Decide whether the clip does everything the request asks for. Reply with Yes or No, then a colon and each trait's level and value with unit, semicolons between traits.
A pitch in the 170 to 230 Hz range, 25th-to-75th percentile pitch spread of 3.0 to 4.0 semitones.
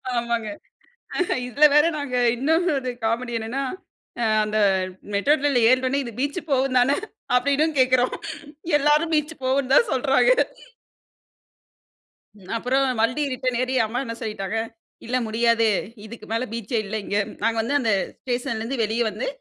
No: very high, 250 Hz; average, 3.3 semitones